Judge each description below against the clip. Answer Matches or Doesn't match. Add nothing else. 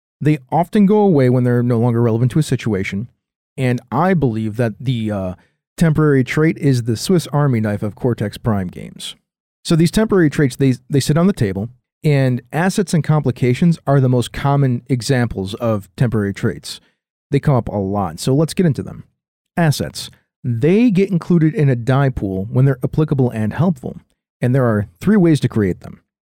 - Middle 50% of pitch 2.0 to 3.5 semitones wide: Doesn't match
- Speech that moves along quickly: Doesn't match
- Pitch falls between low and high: Doesn't match